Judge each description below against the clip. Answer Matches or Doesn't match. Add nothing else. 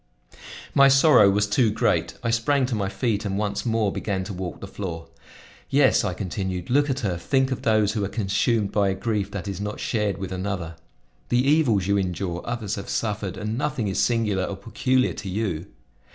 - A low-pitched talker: Matches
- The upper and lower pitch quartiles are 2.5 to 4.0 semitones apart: Matches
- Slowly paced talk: Doesn't match